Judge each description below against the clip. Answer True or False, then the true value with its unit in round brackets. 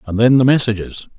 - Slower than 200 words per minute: False (205 wpm)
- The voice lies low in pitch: True (115 Hz)